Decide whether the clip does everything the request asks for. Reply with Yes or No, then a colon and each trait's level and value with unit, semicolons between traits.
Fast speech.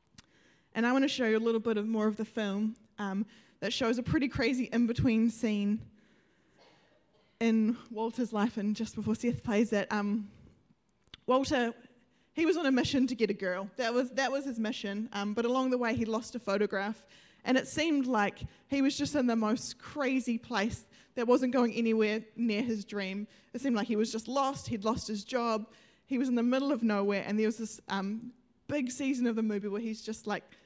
Yes: fast, 210 wpm